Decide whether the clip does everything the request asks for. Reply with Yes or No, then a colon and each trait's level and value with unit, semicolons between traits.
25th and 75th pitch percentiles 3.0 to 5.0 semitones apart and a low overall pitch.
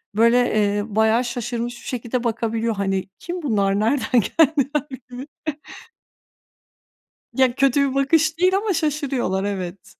No: average, 4.7 semitones; high, 240 Hz